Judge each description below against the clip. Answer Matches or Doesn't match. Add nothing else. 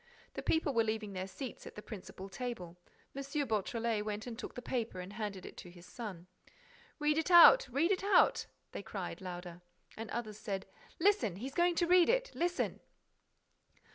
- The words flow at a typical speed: Matches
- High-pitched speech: Matches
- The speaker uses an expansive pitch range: Matches